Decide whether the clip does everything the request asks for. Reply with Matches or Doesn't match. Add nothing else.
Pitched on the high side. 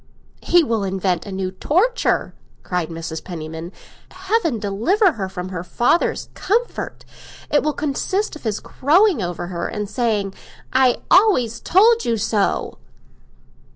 Matches